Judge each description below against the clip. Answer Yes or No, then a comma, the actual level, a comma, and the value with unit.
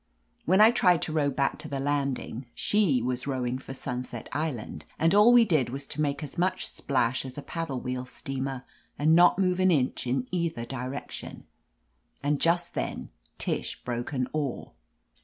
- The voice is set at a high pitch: No, medium, 140 Hz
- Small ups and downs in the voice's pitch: No, average, 4.6 semitones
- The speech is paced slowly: No, average, 175 wpm